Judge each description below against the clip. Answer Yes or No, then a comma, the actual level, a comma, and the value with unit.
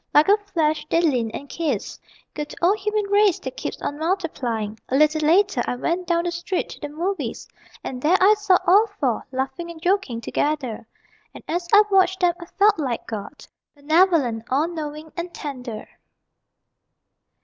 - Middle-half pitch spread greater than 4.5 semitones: Yes, average, 5.3 semitones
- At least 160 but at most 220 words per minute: Yes, average, 170 wpm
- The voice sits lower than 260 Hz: No, very high, 320 Hz